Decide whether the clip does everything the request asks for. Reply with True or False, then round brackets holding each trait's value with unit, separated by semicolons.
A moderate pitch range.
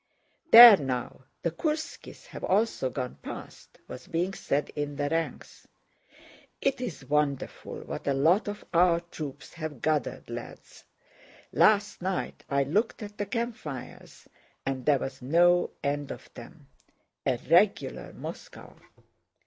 False (6.4 semitones)